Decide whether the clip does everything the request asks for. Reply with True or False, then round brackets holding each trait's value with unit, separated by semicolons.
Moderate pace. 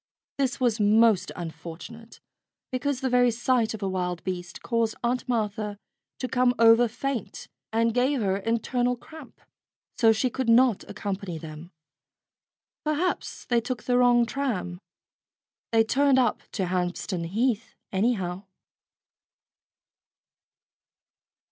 False (120 wpm)